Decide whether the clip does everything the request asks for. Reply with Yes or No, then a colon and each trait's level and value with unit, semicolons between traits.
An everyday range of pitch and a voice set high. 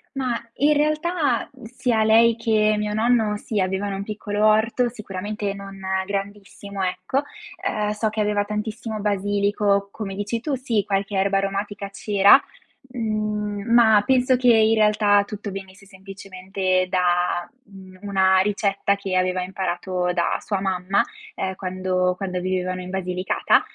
No: narrow, 2.2 semitones; high, 200 Hz